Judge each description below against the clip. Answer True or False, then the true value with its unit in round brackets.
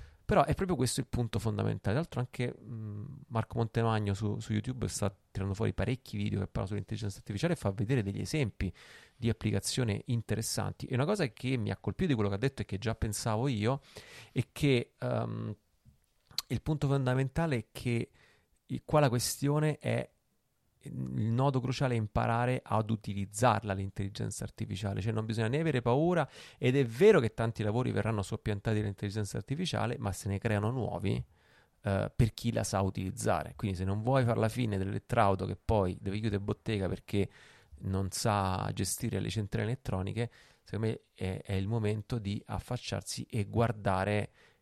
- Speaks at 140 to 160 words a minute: False (170 wpm)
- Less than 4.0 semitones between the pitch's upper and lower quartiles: True (3.6 semitones)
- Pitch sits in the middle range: False (110 Hz)